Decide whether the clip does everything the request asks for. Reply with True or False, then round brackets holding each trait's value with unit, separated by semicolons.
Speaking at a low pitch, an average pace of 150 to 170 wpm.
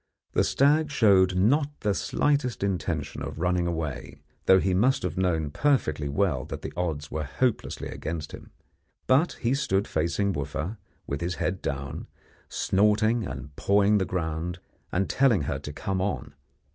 True (95 Hz; 160 wpm)